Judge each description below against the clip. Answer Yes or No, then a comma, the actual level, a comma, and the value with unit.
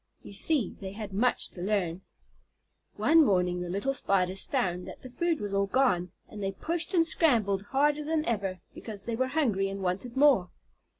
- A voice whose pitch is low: No, high, 205 Hz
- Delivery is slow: No, average, 185 wpm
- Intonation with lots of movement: Yes, wide, 6.2 semitones